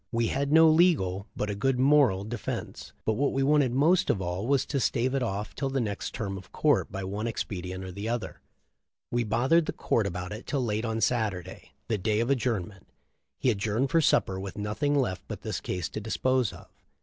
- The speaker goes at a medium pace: No, fast, 210 wpm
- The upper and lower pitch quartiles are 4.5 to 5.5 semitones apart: Yes, average, 5.2 semitones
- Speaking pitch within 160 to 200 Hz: No, low, 115 Hz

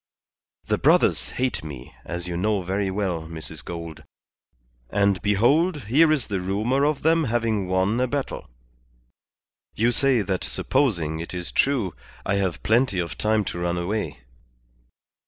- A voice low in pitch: Yes, low, 100 Hz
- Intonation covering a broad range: Yes, wide, 5.9 semitones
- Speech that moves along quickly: No, average, 150 wpm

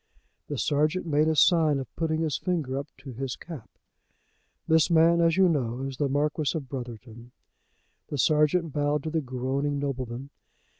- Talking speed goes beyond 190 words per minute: No, average, 165 wpm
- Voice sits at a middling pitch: Yes, medium, 145 Hz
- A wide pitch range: No, average, 3.2 semitones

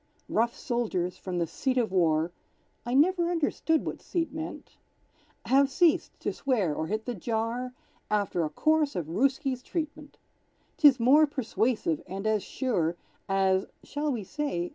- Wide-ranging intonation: Yes, wide, 7.3 semitones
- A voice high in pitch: Yes, high, 240 Hz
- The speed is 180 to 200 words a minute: No, average, 150 wpm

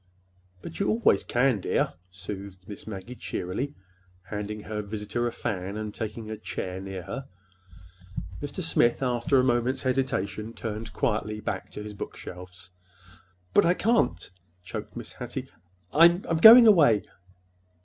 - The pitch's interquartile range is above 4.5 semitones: Yes, average, 5.1 semitones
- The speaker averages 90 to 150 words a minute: Yes, average, 140 wpm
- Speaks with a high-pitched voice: No, low, 110 Hz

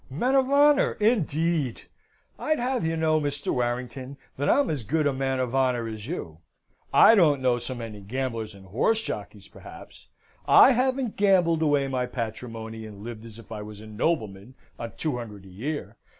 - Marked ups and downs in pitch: Yes, wide, 6.4 semitones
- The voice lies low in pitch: Yes, low, 130 Hz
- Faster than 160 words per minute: Yes, average, 185 wpm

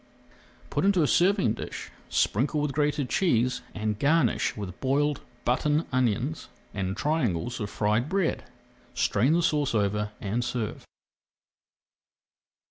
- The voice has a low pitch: Yes, low, 125 Hz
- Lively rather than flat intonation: Yes, wide, 5.9 semitones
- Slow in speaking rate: Yes, slow, 125 wpm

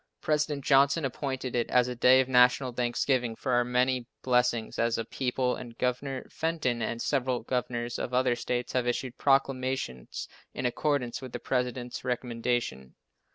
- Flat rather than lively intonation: Yes, narrow, 1.5 semitones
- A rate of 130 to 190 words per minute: Yes, average, 155 wpm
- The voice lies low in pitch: Yes, low, 125 Hz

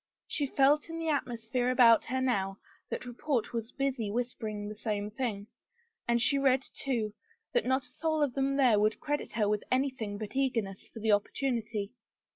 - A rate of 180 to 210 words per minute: Yes, average, 190 wpm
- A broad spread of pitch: No, average, 4.1 semitones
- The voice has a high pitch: Yes, high, 245 Hz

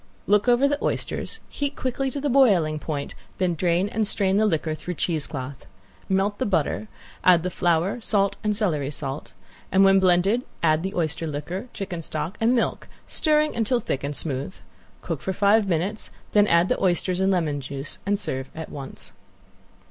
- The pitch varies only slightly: No, average, 5.0 semitones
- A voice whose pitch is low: No, medium, 185 Hz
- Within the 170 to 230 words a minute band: Yes, average, 180 wpm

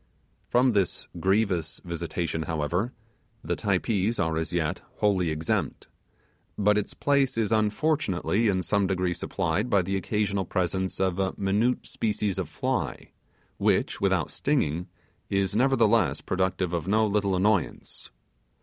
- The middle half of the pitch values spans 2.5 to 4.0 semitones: Yes, average, 3.3 semitones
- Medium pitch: No, very low, 95 Hz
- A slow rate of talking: Yes, slow, 130 wpm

